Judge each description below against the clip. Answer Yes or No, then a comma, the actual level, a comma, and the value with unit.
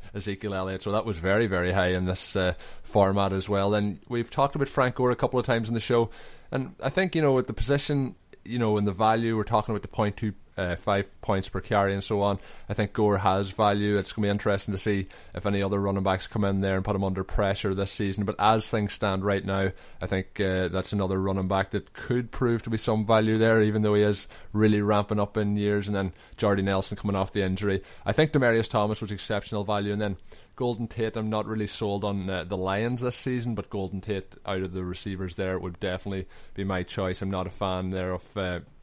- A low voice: Yes, low, 100 Hz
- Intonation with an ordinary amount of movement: No, narrow, 2.3 semitones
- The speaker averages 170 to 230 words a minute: No, fast, 250 wpm